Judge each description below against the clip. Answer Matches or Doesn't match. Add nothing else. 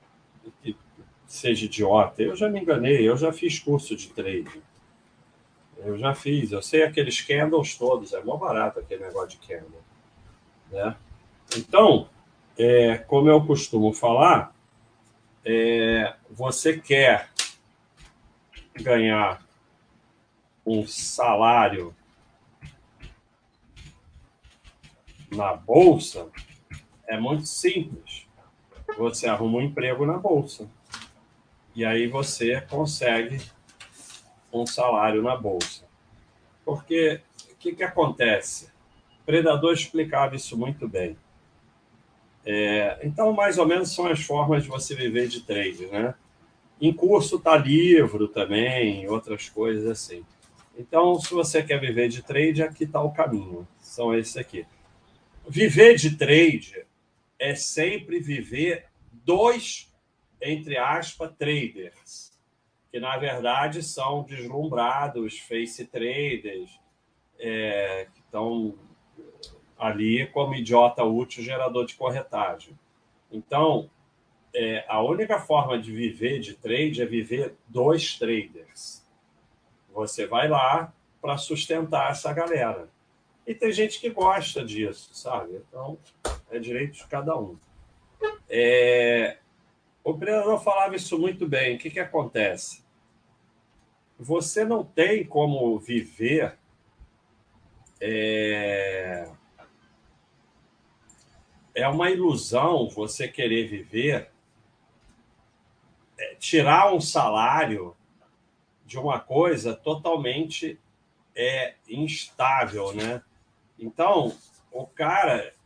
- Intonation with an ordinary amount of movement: Doesn't match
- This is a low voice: Matches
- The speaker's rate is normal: Doesn't match